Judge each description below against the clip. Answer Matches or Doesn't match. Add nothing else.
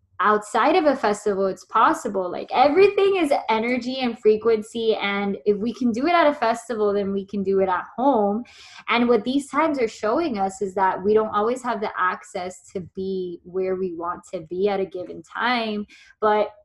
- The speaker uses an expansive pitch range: Doesn't match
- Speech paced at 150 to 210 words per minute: Matches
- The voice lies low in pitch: Doesn't match